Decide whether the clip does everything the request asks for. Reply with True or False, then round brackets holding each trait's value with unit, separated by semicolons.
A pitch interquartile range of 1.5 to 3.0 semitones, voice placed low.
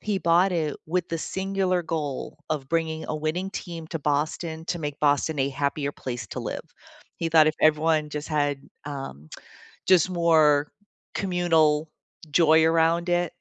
False (2.4 semitones; 160 Hz)